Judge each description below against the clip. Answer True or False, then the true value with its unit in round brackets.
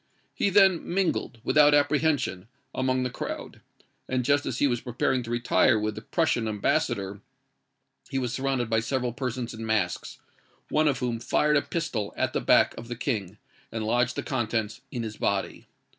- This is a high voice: False (120 Hz)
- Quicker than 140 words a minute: True (175 wpm)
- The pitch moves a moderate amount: True (4.0 semitones)